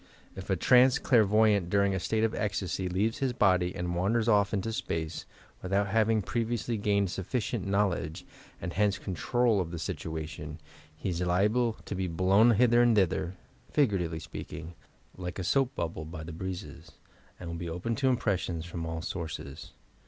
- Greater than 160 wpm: Yes, average, 180 wpm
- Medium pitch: No, very low, 95 Hz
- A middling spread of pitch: Yes, average, 4.3 semitones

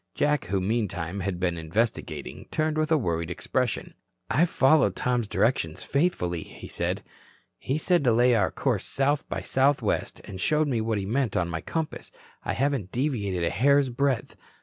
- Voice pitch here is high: No, low, 120 Hz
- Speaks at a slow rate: No, average, 175 wpm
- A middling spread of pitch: No, wide, 7.3 semitones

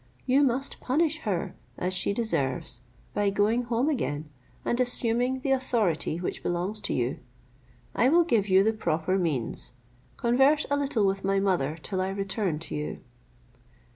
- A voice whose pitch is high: Yes, high, 205 Hz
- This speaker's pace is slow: No, average, 160 wpm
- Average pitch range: No, wide, 6.1 semitones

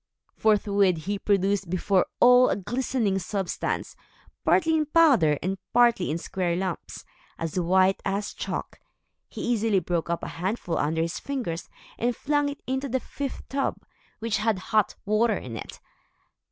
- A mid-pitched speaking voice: No, high, 200 Hz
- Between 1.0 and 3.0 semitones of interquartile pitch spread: No, average, 5.0 semitones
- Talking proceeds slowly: No, average, 155 wpm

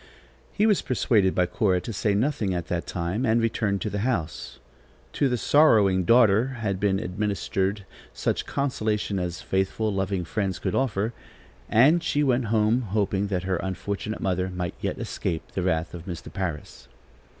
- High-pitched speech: No, low, 100 Hz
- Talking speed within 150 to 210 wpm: Yes, average, 165 wpm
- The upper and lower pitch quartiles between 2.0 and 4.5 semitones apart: Yes, average, 3.6 semitones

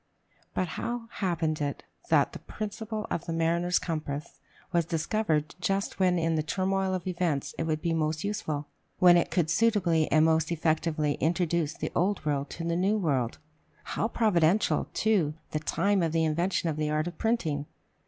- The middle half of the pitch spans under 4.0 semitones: Yes, average, 3.4 semitones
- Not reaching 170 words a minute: No, average, 175 wpm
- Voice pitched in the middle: Yes, medium, 170 Hz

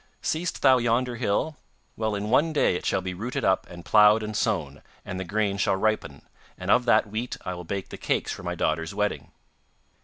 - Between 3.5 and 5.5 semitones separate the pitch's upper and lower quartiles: Yes, average, 3.9 semitones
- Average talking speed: No, fast, 210 wpm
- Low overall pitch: Yes, low, 105 Hz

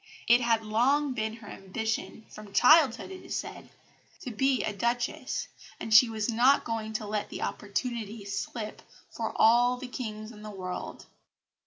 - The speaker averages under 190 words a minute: Yes, average, 165 wpm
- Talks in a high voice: Yes, high, 225 Hz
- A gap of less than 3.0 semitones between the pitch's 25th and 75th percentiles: Yes, narrow, 2.6 semitones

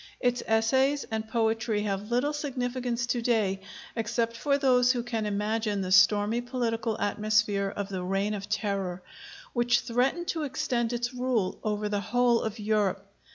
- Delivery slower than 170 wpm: Yes, average, 155 wpm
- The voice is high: Yes, high, 225 Hz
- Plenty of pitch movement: No, average, 3.0 semitones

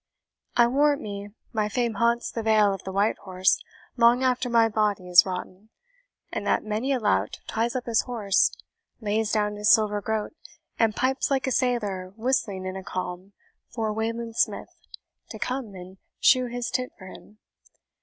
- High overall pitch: Yes, high, 220 Hz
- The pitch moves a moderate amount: Yes, average, 3.2 semitones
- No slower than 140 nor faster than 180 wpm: Yes, average, 170 wpm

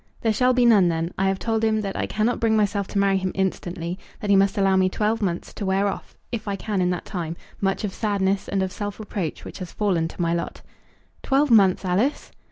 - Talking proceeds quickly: Yes, fast, 240 wpm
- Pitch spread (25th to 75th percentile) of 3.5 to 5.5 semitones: No, narrow, 2.5 semitones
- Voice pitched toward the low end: No, high, 195 Hz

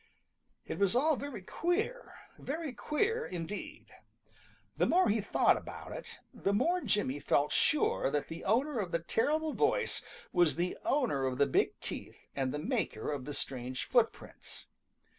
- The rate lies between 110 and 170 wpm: Yes, average, 160 wpm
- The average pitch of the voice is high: Yes, high, 205 Hz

